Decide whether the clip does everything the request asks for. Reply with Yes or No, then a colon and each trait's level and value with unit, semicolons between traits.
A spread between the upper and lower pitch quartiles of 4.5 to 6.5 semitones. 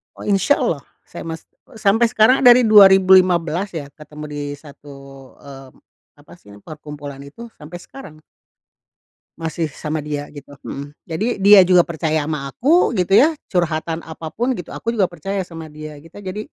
Yes: average, 4.9 semitones